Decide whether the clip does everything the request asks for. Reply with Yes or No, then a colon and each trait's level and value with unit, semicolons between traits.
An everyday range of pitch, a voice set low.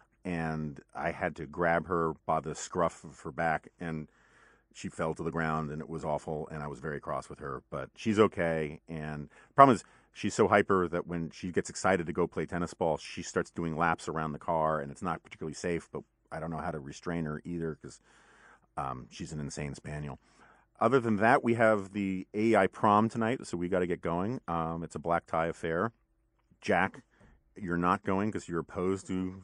Yes: average, 3.5 semitones; very low, 85 Hz